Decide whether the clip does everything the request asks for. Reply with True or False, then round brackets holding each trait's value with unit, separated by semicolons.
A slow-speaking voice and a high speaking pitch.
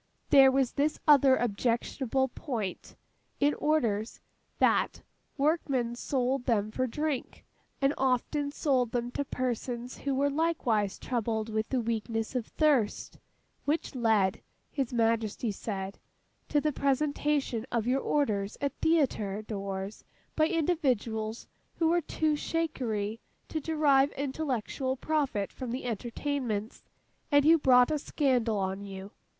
True (130 wpm; 255 Hz)